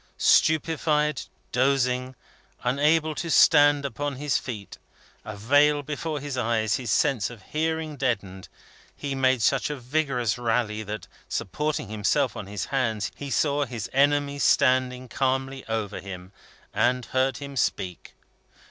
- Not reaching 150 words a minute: Yes, slow, 135 wpm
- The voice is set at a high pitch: No, low, 130 Hz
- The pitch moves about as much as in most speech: Yes, average, 4.2 semitones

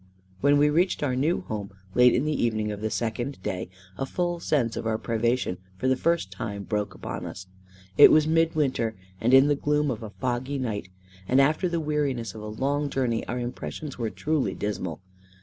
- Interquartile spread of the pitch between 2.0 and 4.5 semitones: No, average, 5.2 semitones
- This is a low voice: Yes, low, 125 Hz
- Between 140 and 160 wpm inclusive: No, average, 200 wpm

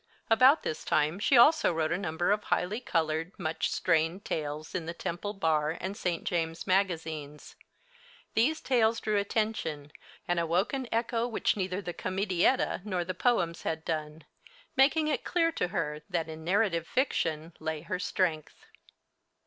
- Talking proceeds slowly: No, average, 155 wpm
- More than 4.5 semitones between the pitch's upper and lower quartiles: Yes, average, 5.0 semitones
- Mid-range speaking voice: Yes, medium, 175 Hz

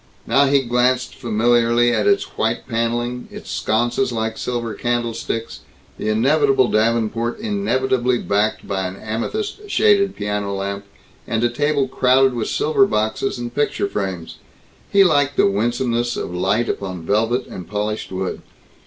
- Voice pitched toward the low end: Yes, low, 120 Hz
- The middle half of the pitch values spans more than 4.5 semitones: No, average, 3.6 semitones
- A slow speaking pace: No, average, 145 wpm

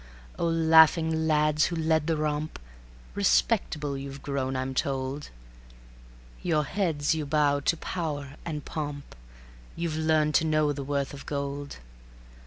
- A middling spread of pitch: No, narrow, 2.1 semitones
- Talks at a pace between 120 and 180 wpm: Yes, slow, 135 wpm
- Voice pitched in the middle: Yes, medium, 150 Hz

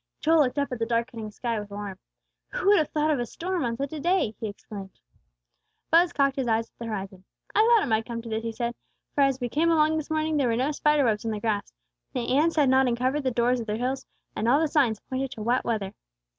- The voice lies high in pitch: Yes, very high, 255 Hz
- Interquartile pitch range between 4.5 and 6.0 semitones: Yes, average, 4.9 semitones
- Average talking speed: No, fast, 260 wpm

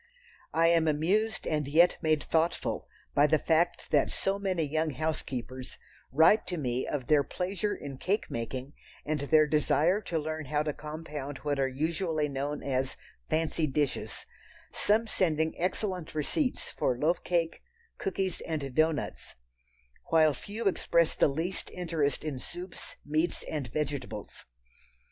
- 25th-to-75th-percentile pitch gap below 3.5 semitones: Yes, average, 3.0 semitones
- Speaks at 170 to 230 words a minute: No, average, 145 wpm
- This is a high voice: No, medium, 155 Hz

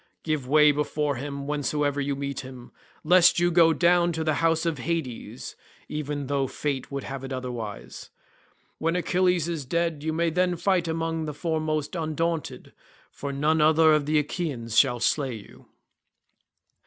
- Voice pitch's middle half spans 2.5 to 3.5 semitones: Yes, average, 2.9 semitones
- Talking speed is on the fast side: No, average, 160 wpm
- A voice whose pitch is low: No, medium, 150 Hz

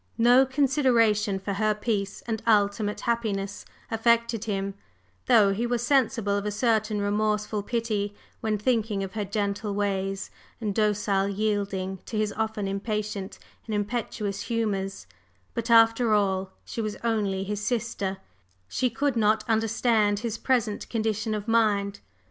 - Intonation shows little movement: Yes, narrow, 2.2 semitones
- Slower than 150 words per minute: Yes, average, 140 wpm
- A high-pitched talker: Yes, high, 215 Hz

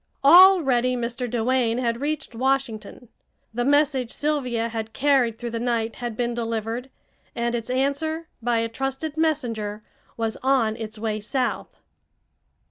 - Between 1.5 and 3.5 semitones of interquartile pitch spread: Yes, average, 3.0 semitones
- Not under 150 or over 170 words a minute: No, slow, 135 wpm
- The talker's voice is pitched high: Yes, high, 240 Hz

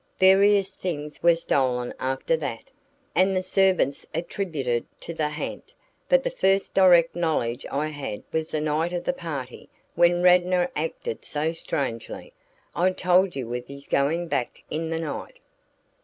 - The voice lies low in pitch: No, medium, 165 Hz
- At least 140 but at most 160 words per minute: Yes, average, 155 wpm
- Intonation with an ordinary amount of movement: Yes, average, 4.5 semitones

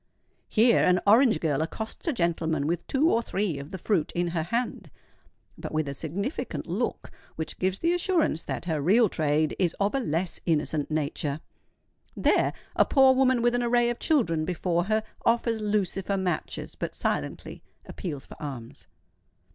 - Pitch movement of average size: No, wide, 6.7 semitones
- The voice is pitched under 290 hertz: Yes, medium, 185 Hz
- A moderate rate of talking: Yes, average, 165 wpm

